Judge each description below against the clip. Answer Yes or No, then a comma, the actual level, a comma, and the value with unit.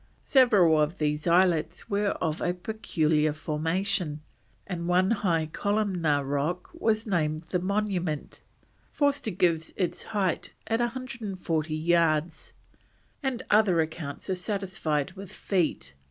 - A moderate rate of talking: No, slow, 120 wpm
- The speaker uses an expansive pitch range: No, average, 4.4 semitones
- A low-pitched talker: No, medium, 180 Hz